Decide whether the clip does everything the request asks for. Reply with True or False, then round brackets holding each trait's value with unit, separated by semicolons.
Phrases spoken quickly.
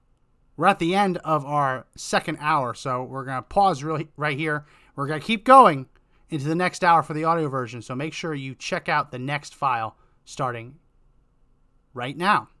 False (195 wpm)